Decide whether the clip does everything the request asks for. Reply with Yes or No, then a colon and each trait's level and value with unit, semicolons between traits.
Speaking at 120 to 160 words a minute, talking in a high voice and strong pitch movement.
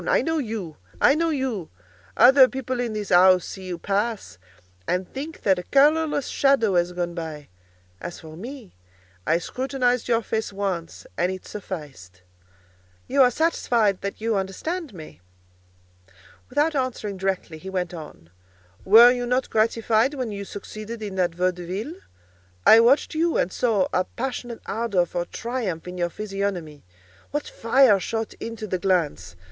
Yes: average, 155 wpm; high, 210 Hz; wide, 5.7 semitones